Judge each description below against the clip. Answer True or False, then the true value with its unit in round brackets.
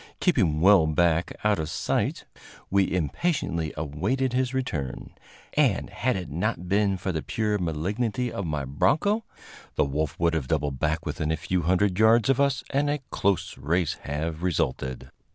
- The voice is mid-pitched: False (90 Hz)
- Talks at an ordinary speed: True (165 wpm)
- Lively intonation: True (6.1 semitones)